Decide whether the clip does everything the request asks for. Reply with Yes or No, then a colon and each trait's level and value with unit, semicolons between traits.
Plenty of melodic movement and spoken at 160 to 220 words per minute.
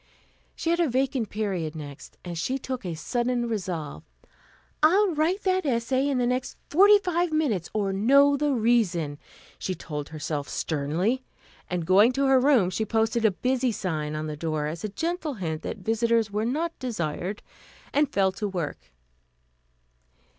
Yes: wide, 7.7 semitones; average, 165 wpm